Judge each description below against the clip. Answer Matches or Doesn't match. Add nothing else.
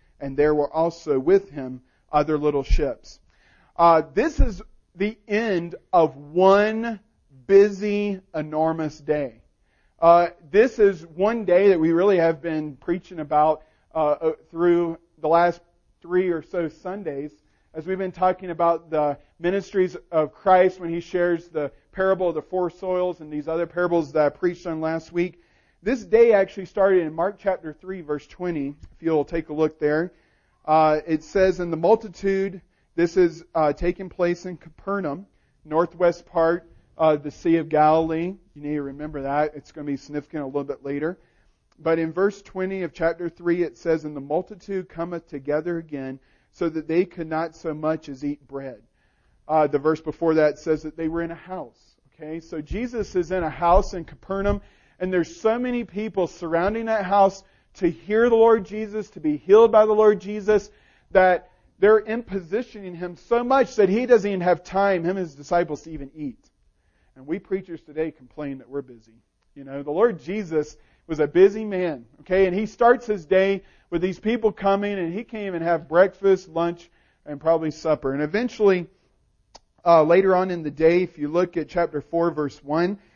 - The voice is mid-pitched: Matches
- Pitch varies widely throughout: Doesn't match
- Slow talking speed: Doesn't match